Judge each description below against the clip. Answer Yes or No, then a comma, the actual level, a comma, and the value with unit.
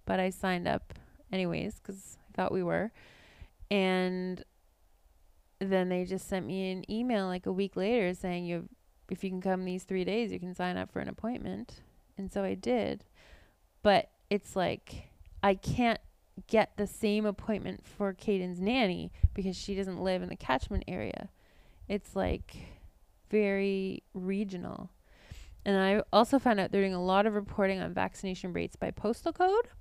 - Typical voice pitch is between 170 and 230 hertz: Yes, high, 190 Hz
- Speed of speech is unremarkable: Yes, average, 165 wpm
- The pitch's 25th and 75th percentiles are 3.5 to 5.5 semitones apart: No, average, 2.7 semitones